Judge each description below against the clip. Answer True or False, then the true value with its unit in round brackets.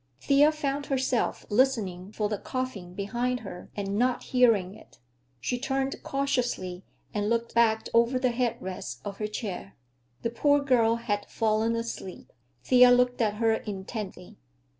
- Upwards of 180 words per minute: False (150 wpm)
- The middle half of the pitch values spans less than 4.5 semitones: True (3.6 semitones)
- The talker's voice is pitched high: True (230 Hz)